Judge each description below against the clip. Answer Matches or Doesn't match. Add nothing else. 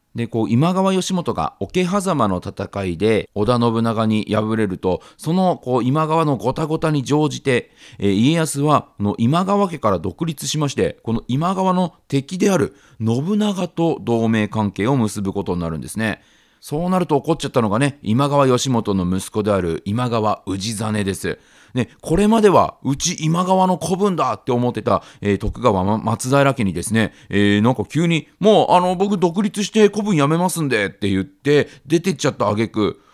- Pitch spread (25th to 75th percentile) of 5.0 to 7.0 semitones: Doesn't match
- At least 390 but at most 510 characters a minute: Doesn't match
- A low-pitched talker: Matches